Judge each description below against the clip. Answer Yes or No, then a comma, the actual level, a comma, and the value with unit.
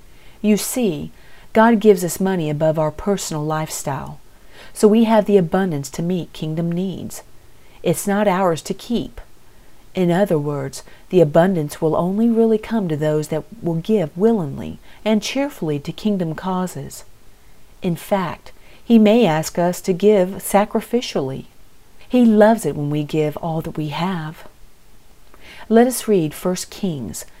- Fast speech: No, average, 150 wpm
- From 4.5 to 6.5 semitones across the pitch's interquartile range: Yes, average, 5.1 semitones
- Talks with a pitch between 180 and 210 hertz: Yes, medium, 185 Hz